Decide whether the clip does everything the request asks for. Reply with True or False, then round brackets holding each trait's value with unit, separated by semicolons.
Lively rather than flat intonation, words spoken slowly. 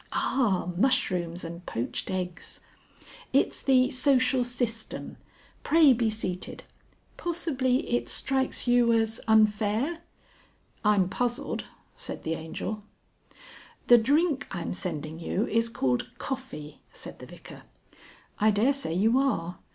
True (6.1 semitones; 115 wpm)